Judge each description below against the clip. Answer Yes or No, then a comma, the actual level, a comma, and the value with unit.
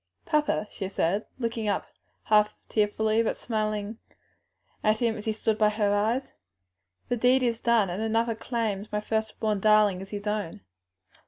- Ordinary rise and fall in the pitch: No, narrow, 1.6 semitones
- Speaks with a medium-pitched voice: No, high, 215 Hz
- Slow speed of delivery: No, average, 170 wpm